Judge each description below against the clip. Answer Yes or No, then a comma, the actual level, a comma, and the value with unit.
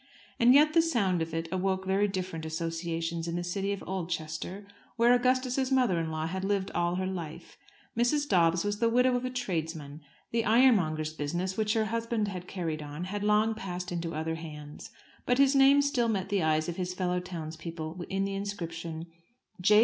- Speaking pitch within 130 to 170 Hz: No, medium, 185 Hz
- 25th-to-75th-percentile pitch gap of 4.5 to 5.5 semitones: Yes, average, 5.1 semitones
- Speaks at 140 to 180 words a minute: No, average, 190 wpm